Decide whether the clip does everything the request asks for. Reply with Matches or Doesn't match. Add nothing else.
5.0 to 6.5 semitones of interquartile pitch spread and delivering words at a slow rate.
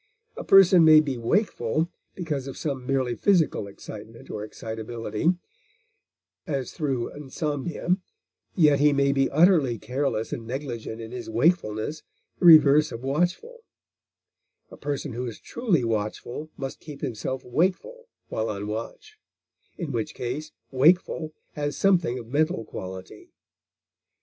Matches